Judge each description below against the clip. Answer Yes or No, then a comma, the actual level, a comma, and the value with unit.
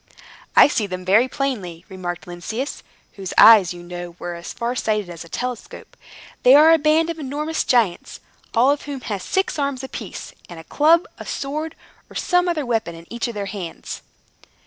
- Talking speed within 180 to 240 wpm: Yes, average, 190 wpm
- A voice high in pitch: Yes, high, 235 Hz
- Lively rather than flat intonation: Yes, wide, 8.1 semitones